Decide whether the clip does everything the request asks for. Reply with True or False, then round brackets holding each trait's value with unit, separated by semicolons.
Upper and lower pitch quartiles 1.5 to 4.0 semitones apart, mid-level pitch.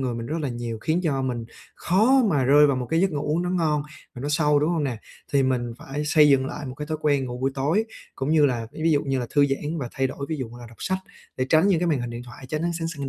True (3.4 semitones; 145 Hz)